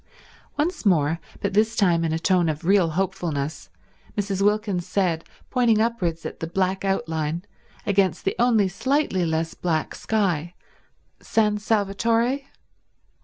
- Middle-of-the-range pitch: No, high, 195 Hz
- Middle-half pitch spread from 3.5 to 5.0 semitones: Yes, average, 4.3 semitones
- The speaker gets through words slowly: Yes, slow, 130 wpm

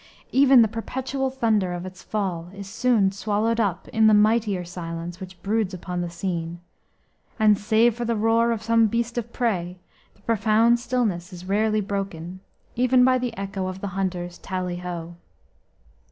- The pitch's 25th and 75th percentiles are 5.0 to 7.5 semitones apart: No, average, 4.0 semitones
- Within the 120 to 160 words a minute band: No, average, 170 wpm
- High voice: Yes, high, 205 Hz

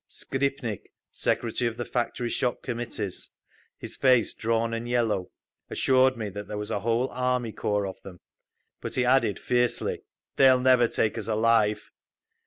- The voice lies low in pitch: Yes, low, 115 Hz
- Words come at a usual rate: Yes, average, 155 wpm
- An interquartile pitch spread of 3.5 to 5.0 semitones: No, average, 2.9 semitones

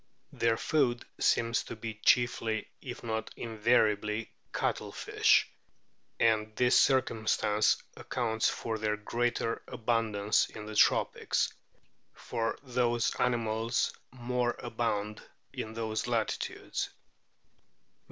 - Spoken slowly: Yes, slow, 95 wpm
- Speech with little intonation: Yes, narrow, 1.8 semitones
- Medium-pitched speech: No, low, 115 Hz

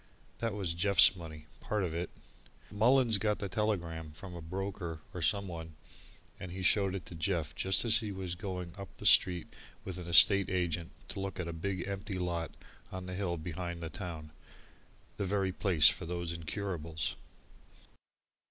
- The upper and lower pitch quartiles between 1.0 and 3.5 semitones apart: Yes, average, 2.8 semitones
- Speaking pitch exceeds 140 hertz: No, very low, 90 Hz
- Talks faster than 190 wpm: No, average, 170 wpm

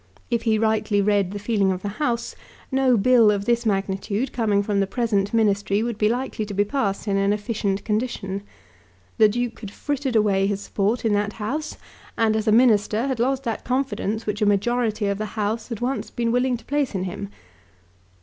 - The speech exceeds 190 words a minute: Yes, average, 200 wpm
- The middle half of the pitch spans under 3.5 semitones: Yes, average, 2.9 semitones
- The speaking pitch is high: Yes, high, 215 Hz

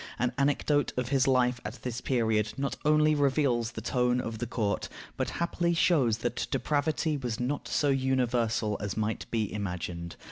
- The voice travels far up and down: No, average, 4.1 semitones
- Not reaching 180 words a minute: Yes, average, 170 wpm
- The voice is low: Yes, low, 125 Hz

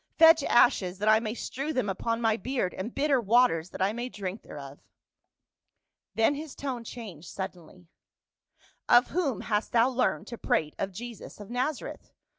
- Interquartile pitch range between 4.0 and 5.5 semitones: Yes, average, 4.7 semitones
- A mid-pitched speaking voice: No, high, 230 Hz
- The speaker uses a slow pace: No, average, 175 wpm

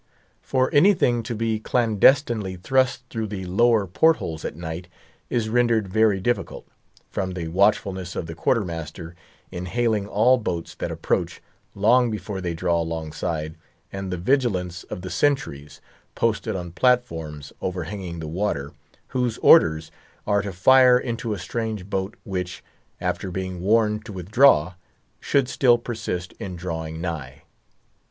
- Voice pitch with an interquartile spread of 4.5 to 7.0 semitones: Yes, average, 5.1 semitones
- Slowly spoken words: No, average, 145 wpm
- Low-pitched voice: Yes, very low, 95 Hz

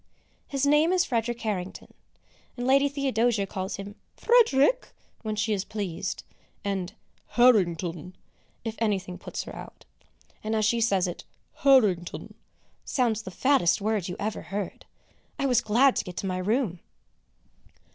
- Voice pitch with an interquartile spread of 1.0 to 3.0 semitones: No, average, 5.2 semitones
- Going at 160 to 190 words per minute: No, average, 145 wpm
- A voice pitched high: Yes, high, 215 Hz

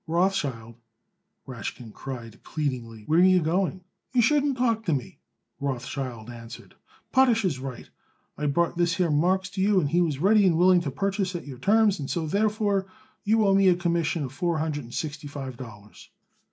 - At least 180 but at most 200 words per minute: Yes, average, 185 wpm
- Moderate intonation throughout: No, wide, 6.2 semitones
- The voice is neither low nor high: Yes, medium, 170 Hz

